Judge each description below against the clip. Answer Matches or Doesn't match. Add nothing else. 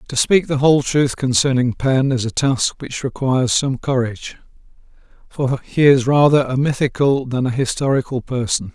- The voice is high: Doesn't match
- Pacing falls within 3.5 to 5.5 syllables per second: Matches